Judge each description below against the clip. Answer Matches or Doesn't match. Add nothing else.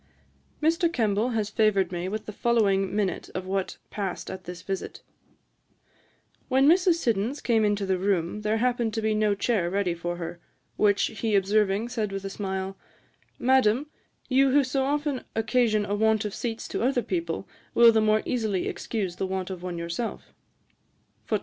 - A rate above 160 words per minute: Matches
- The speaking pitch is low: Doesn't match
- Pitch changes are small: Doesn't match